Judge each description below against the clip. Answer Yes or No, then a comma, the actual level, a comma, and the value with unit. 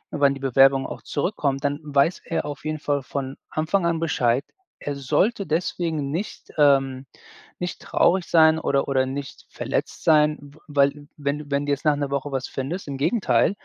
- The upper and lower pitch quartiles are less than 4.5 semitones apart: Yes, narrow, 2.4 semitones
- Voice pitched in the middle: Yes, medium, 145 Hz